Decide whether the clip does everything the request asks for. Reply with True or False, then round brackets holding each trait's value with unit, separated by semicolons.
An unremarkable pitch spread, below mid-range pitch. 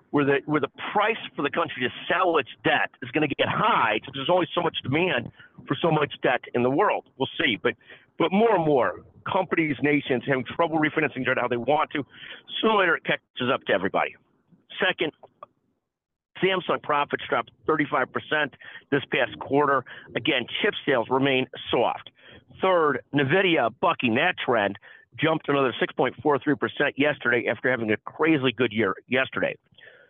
False (3.5 semitones; 145 Hz)